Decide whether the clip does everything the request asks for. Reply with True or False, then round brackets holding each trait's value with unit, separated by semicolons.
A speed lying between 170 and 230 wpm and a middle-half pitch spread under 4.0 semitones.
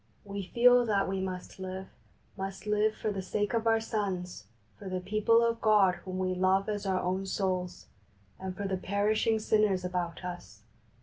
True (180 wpm; 2.5 semitones)